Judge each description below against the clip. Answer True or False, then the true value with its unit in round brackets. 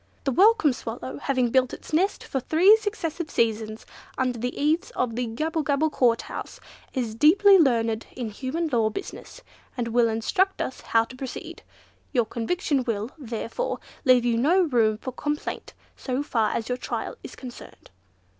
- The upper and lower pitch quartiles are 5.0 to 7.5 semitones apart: True (5.3 semitones)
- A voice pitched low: False (255 Hz)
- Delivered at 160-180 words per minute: True (165 wpm)